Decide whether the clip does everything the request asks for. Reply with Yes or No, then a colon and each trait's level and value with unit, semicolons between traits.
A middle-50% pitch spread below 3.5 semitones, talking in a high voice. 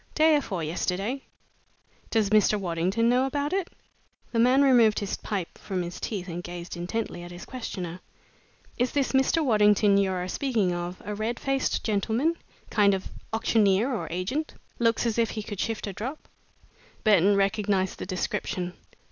No: average, 4.5 semitones; high, 210 Hz